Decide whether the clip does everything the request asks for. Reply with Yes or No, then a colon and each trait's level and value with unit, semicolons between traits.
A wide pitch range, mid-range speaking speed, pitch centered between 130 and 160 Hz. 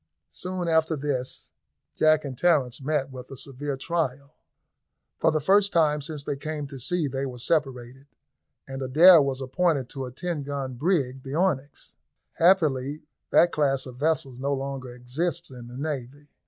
No: average, 3.2 semitones; average, 165 wpm; medium, 140 Hz